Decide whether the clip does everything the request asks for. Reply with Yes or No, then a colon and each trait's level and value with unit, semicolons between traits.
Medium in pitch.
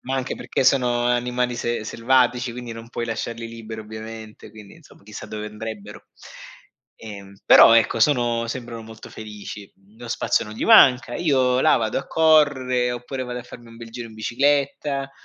No: low, 120 Hz